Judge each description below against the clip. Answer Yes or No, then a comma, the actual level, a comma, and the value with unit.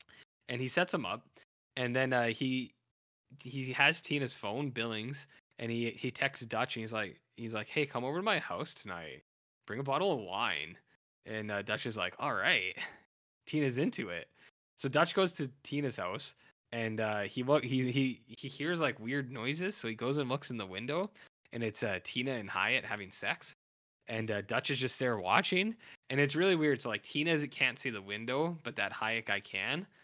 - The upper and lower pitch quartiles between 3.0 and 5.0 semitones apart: Yes, average, 4.0 semitones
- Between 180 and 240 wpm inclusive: Yes, average, 200 wpm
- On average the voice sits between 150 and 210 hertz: No, low, 130 Hz